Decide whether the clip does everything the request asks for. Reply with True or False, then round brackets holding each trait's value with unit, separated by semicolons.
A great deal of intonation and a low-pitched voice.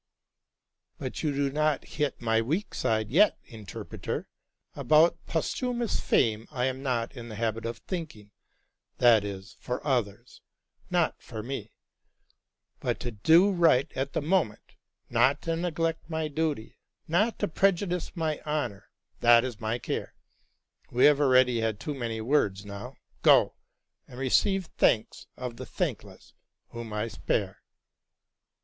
True (5.9 semitones; 130 Hz)